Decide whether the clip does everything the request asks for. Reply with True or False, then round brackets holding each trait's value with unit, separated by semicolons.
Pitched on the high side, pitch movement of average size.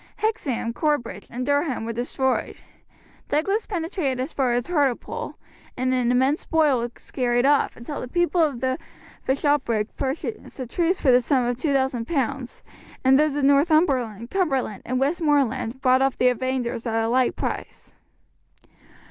True (265 Hz; 3.2 semitones)